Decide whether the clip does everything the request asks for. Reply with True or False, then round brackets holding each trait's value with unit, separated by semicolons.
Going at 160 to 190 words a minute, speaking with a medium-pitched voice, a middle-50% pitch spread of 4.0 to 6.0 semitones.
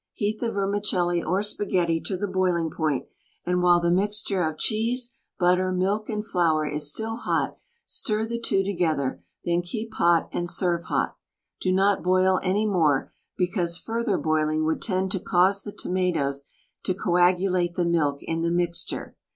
False (165 wpm; 180 Hz; 2.8 semitones)